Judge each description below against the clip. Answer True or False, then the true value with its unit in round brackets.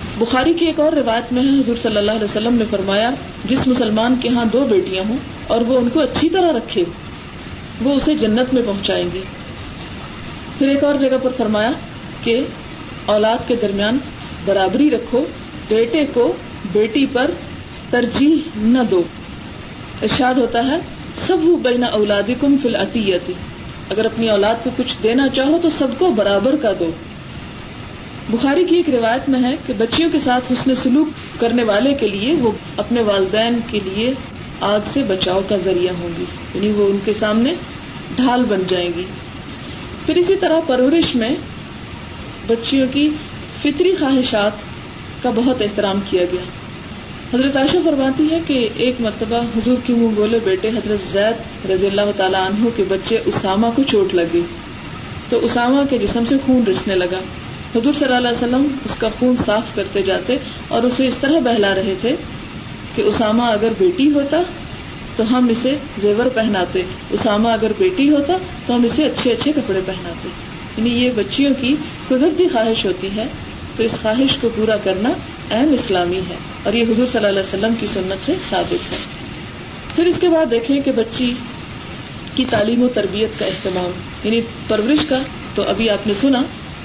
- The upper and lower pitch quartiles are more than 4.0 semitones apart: True (4.5 semitones)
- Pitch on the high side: True (235 Hz)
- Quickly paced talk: False (170 wpm)